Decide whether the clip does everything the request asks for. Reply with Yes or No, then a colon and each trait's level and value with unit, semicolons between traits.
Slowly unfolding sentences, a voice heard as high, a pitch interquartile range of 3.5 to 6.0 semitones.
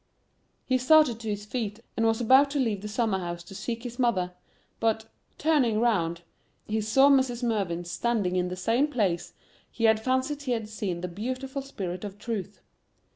No: average, 180 wpm; high, 225 Hz; average, 4.7 semitones